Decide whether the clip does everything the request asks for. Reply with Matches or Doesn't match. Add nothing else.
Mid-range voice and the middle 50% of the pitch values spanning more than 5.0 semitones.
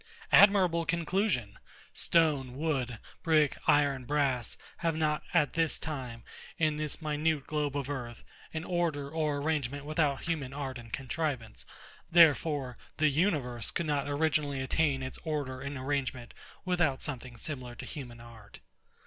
Doesn't match